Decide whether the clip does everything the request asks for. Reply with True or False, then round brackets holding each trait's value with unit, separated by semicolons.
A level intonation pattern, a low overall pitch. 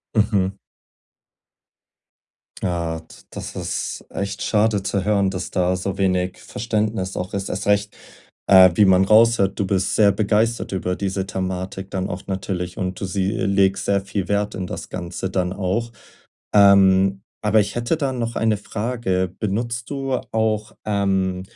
True (2.2 semitones; 100 Hz)